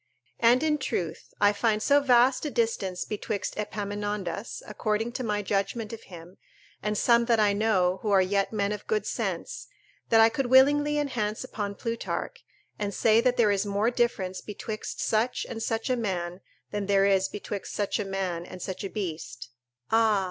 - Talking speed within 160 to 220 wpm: Yes, average, 180 wpm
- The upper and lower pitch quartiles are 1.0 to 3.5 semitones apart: Yes, average, 3.0 semitones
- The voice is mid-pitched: No, high, 210 Hz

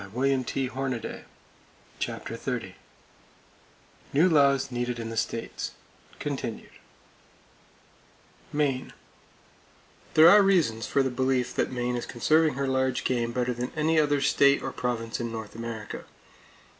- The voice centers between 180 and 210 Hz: No, low, 130 Hz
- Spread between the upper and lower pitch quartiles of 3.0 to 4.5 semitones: No, narrow, 2.6 semitones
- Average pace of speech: No, slow, 125 wpm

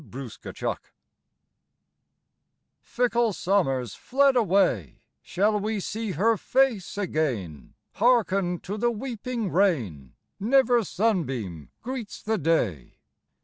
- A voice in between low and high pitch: No, high, 200 Hz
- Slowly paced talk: Yes, slow, 100 wpm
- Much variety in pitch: Yes, wide, 8.8 semitones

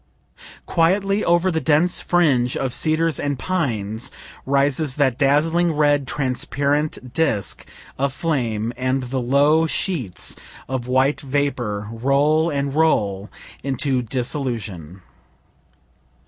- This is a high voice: No, medium, 140 Hz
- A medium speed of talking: No, slow, 105 wpm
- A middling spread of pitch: Yes, average, 4.1 semitones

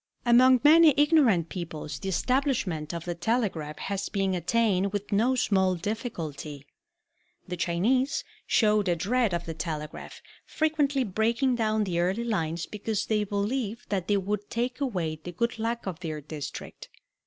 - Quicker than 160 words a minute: No, average, 155 wpm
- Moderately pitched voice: No, high, 205 Hz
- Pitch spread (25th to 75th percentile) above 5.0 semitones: Yes, wide, 5.6 semitones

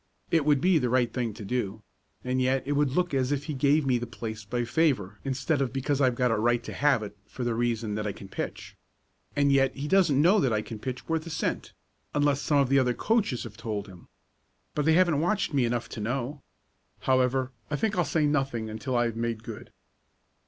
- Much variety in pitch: No, average, 3.7 semitones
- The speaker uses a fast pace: Yes, fast, 230 wpm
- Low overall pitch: Yes, low, 130 Hz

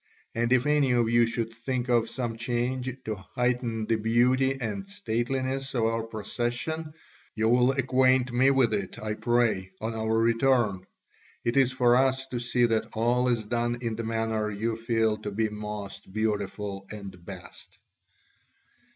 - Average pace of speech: Yes, average, 160 wpm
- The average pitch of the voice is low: Yes, low, 115 Hz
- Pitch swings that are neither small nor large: No, narrow, 2.3 semitones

